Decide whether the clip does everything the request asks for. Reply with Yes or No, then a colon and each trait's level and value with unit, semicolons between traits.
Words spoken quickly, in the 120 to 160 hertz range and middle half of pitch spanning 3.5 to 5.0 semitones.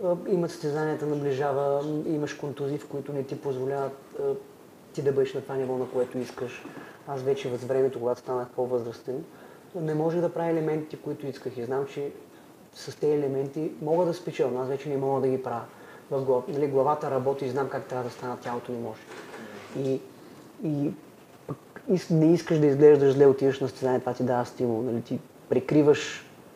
No: fast, 180 wpm; medium, 140 Hz; average, 2.9 semitones